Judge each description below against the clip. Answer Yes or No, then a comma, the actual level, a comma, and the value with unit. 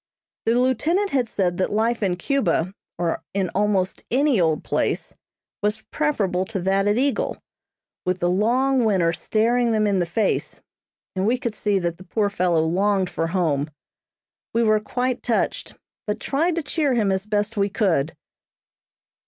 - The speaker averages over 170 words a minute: No, average, 165 wpm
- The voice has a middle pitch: No, high, 210 Hz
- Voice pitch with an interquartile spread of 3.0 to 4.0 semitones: No, average, 4.6 semitones